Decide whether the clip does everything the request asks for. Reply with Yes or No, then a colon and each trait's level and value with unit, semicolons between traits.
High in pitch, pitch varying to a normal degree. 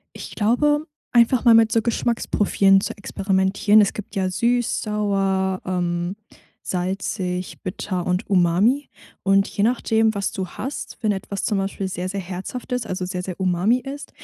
Yes: high, 195 Hz; average, 3.3 semitones